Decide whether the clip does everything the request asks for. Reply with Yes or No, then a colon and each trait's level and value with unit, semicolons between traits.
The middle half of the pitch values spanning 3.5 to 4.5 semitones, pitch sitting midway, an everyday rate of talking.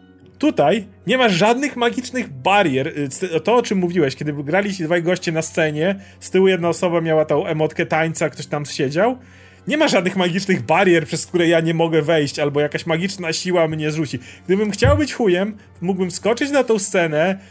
No: average, 4.0 semitones; medium, 170 Hz; fast, 185 wpm